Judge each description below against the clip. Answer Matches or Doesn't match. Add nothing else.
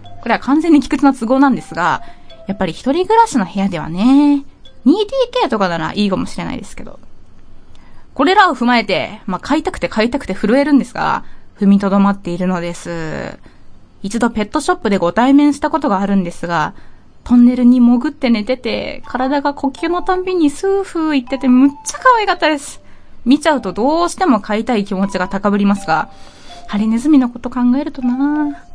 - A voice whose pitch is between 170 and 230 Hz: Doesn't match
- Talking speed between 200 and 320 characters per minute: Doesn't match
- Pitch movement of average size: Doesn't match